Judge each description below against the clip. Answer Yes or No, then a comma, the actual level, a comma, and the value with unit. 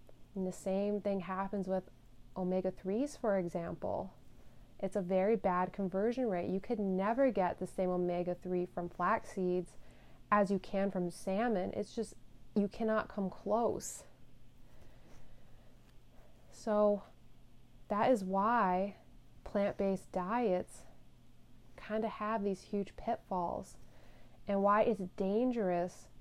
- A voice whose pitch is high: Yes, high, 195 Hz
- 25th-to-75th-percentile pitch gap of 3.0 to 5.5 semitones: No, narrow, 2.4 semitones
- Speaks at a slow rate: Yes, slow, 125 wpm